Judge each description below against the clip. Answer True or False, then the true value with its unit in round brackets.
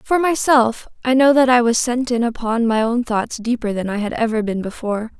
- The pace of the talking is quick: True (230 wpm)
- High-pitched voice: True (235 Hz)